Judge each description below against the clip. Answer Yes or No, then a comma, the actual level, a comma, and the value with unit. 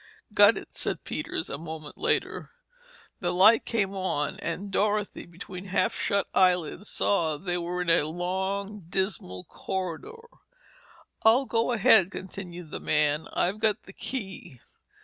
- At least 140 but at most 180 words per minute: Yes, average, 145 wpm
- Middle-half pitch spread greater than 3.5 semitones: No, average, 3.2 semitones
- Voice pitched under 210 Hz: Yes, medium, 185 Hz